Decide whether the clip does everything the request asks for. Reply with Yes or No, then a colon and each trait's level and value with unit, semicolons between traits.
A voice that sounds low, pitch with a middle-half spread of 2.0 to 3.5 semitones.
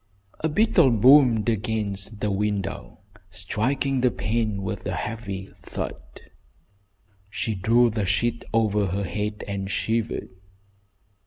Yes: low, 105 Hz; average, 2.9 semitones